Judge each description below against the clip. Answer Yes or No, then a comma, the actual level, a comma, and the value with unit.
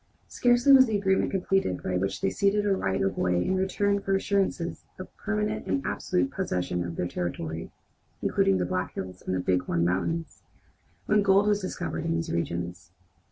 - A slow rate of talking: No, average, 175 wpm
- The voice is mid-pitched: Yes, medium, 170 Hz